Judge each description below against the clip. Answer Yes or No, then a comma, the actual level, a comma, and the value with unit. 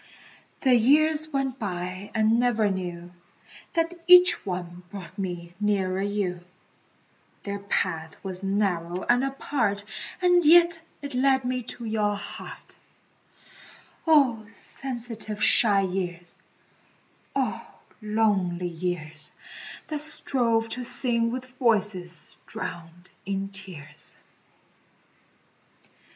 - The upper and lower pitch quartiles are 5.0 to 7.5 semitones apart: Yes, wide, 5.6 semitones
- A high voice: Yes, high, 205 Hz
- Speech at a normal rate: No, slow, 100 wpm